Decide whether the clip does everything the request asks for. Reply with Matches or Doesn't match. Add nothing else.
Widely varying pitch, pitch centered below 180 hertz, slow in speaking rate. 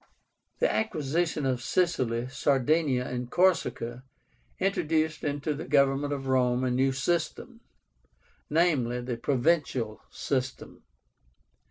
Doesn't match